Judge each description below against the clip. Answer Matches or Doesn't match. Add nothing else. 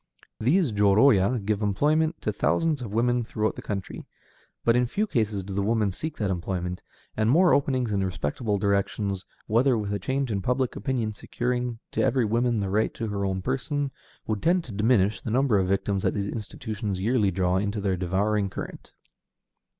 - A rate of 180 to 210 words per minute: Matches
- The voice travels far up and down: Doesn't match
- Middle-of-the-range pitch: Doesn't match